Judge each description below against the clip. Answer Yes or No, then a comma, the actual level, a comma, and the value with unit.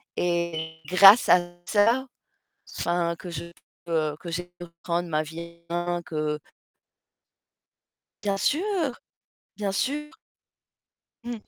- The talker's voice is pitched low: No, medium, 175 Hz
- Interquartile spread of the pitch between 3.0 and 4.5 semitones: Yes, average, 3.4 semitones